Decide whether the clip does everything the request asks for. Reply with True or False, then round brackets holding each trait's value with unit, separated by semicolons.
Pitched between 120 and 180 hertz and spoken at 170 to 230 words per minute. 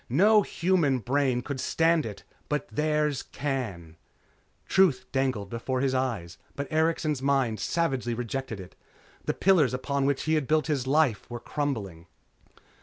False (135 Hz; 145 wpm)